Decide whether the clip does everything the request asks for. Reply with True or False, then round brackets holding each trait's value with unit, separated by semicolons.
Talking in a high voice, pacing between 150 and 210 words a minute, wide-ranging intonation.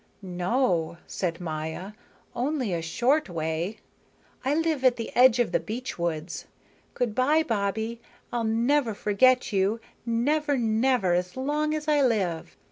False (230 Hz; 140 wpm; 6.2 semitones)